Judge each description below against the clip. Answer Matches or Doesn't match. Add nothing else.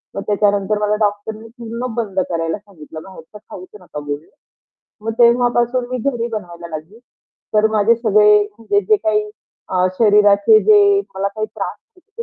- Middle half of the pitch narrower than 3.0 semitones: Doesn't match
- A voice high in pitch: Matches